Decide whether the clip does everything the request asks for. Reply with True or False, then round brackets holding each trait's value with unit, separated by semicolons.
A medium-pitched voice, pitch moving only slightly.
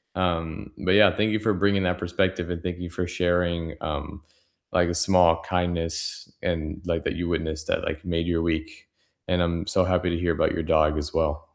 False (85 Hz; 1.6 semitones)